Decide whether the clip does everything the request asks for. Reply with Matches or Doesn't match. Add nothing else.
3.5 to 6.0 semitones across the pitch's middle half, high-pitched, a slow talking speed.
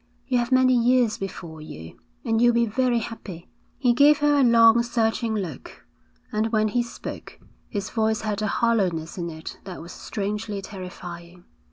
Doesn't match